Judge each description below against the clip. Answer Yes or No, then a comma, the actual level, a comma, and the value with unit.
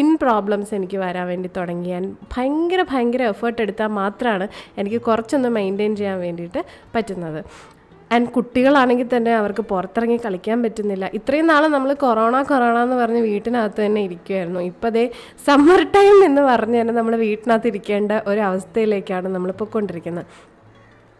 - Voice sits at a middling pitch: No, high, 225 Hz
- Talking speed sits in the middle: No, fast, 135 wpm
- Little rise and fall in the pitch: No, average, 3.8 semitones